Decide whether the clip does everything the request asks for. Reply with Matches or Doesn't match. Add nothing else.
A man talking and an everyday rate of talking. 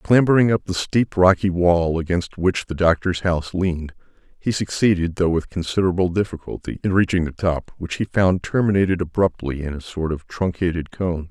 Matches